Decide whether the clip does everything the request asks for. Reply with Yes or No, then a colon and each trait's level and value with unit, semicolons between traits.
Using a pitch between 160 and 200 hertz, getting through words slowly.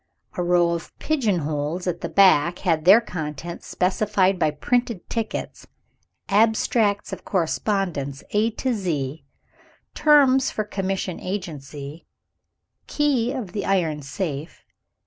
Yes: medium, 185 Hz; slow, 120 wpm